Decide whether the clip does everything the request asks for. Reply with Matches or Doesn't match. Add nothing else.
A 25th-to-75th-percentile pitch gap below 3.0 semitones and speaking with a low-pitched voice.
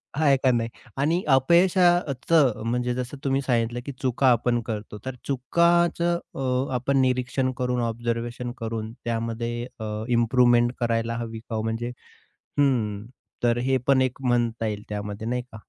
Matches